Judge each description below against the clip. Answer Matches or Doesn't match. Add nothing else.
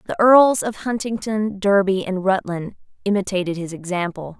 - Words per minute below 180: Matches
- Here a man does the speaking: Doesn't match